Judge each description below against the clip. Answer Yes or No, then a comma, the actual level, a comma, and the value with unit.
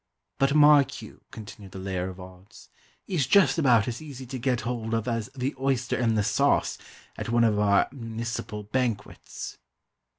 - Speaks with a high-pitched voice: No, low, 115 Hz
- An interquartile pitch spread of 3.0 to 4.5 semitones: Yes, average, 4.1 semitones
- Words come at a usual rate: Yes, average, 170 wpm